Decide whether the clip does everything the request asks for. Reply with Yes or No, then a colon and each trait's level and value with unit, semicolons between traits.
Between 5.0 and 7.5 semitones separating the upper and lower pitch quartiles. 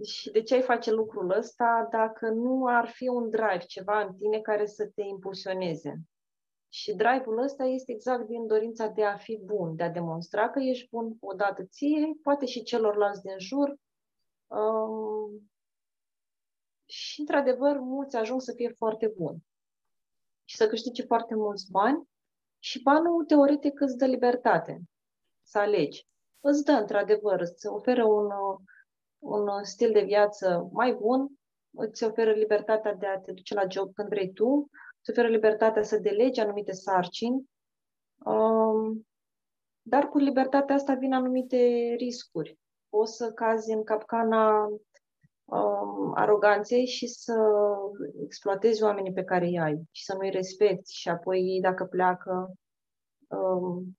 No: average, 3.7 semitones